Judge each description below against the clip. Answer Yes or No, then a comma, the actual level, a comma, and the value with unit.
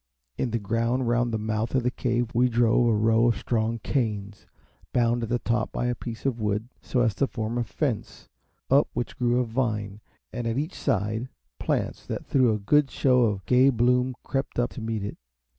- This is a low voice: Yes, low, 120 Hz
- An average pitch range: No, narrow, 2.1 semitones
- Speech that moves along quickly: Yes, fast, 210 wpm